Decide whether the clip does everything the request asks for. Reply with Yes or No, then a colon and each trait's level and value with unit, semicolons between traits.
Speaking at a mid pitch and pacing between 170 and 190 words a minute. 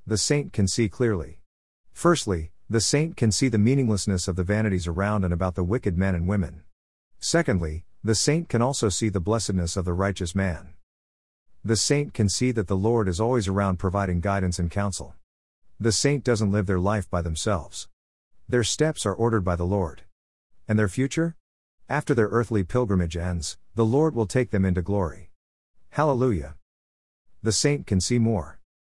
No: low, 100 Hz; average, 175 wpm